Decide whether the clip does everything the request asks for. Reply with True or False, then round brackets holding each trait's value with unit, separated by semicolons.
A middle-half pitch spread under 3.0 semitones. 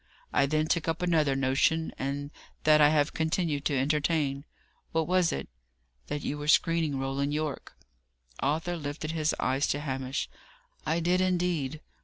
True (2.6 semitones)